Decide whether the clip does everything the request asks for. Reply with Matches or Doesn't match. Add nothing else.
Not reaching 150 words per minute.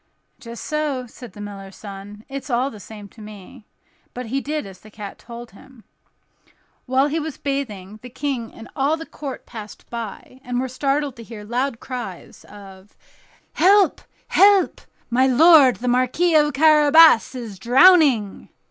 Doesn't match